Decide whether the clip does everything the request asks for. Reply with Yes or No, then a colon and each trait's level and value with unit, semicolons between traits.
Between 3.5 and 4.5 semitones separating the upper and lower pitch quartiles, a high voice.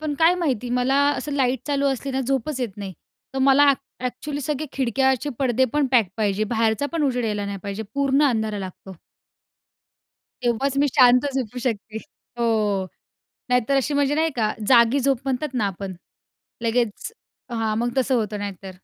Yes: average, 4.1 semitones; very high, 250 Hz